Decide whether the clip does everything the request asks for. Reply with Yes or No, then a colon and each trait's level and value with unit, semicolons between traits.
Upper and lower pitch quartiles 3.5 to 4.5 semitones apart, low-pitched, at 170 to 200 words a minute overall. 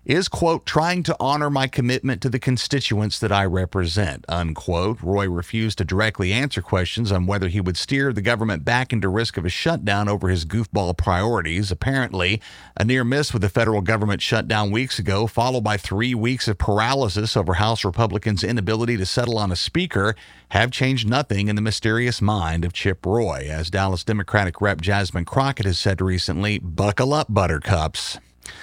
Yes: average, 4.0 semitones; low, 105 Hz; average, 180 wpm